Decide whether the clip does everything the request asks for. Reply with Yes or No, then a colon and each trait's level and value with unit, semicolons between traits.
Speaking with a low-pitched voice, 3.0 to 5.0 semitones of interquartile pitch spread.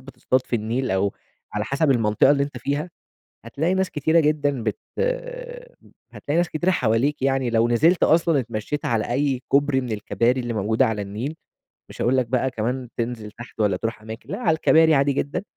Yes: low, 130 Hz; average, 4.3 semitones